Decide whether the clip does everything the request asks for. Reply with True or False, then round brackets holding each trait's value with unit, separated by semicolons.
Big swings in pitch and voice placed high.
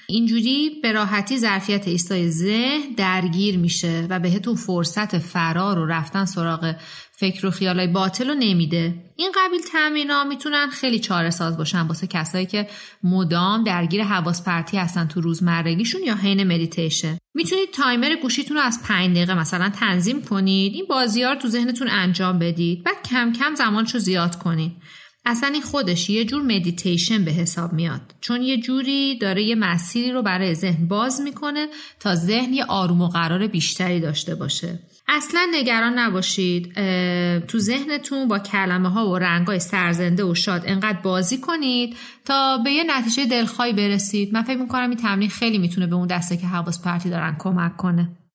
True (5.7 semitones; 195 Hz)